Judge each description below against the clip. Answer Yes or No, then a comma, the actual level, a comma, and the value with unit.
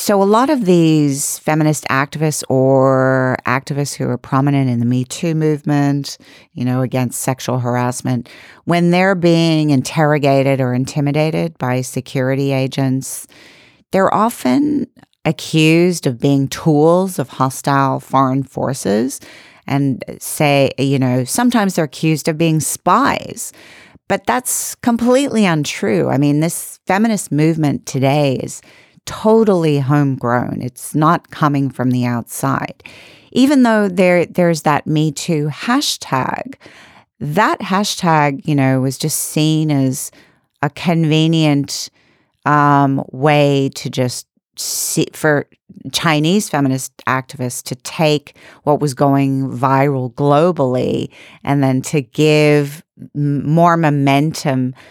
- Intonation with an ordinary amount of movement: Yes, average, 3.8 semitones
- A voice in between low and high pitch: Yes, medium, 145 Hz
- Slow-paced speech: Yes, slow, 120 wpm